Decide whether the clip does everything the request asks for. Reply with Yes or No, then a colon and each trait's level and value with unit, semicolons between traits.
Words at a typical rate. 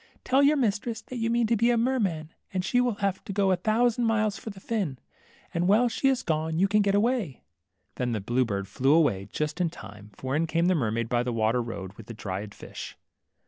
No: fast, 240 wpm